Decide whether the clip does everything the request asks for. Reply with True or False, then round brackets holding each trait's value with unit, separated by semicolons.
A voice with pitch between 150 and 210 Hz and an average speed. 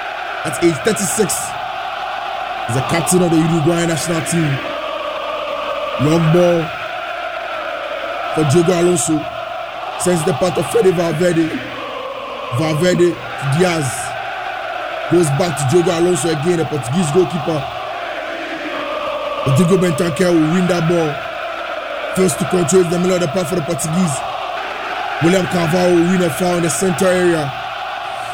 False (185 Hz; 130 wpm)